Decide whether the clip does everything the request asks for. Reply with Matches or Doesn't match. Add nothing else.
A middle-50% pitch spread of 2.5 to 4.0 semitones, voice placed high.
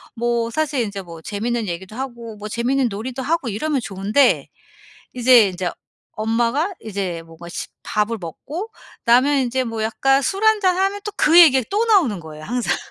Doesn't match